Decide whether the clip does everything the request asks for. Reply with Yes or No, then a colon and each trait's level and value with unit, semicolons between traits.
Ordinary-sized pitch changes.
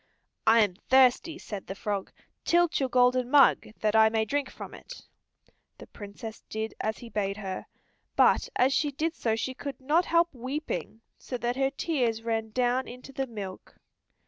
Yes: average, 3.8 semitones